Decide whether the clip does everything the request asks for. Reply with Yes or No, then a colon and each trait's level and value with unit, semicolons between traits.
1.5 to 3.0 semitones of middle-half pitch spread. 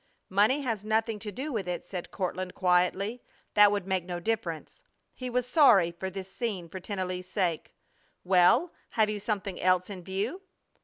No: average, 3.4 semitones